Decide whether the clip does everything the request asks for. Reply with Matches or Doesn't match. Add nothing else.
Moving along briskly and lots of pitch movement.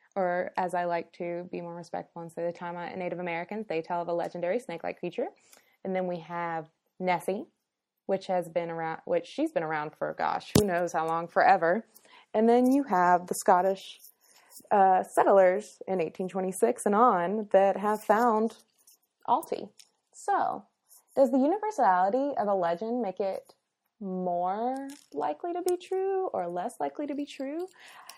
Doesn't match